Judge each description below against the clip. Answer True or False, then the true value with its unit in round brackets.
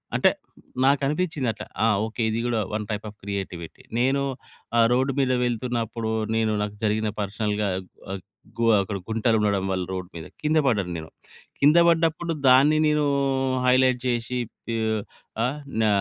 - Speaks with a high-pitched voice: False (115 Hz)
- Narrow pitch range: False (3.9 semitones)